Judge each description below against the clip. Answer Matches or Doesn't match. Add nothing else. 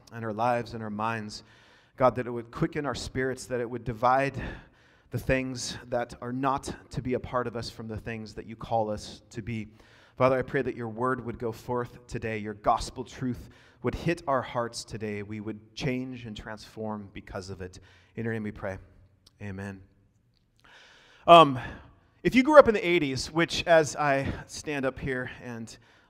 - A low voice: Matches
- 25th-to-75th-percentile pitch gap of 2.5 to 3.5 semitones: Matches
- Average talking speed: Matches